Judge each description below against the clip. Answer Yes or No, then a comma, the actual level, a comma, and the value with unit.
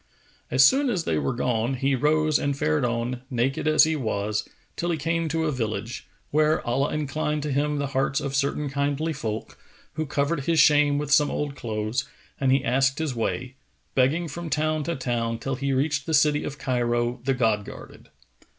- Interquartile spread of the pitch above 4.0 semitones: No, average, 3.5 semitones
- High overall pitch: No, medium, 140 Hz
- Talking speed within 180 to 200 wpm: Yes, average, 195 wpm